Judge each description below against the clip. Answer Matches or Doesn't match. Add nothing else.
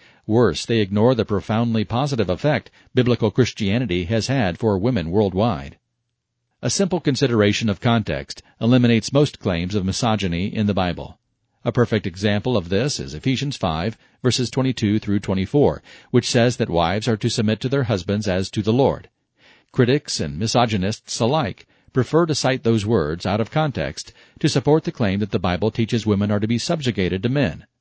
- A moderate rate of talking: Matches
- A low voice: Matches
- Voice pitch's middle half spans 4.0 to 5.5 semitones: Doesn't match